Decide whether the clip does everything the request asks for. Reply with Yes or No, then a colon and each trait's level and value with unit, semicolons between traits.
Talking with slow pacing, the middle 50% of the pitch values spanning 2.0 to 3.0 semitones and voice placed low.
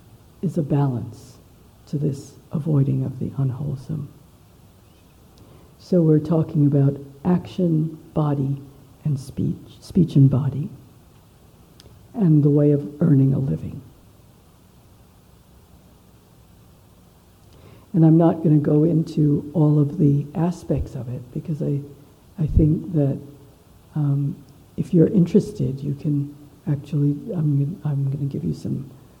No: slow, 120 wpm; narrow, 2.5 semitones; medium, 145 Hz